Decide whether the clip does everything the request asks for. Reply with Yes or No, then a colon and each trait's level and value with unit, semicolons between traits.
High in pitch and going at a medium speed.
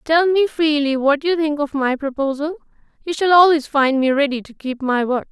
No: very high, 290 Hz; fast, 215 wpm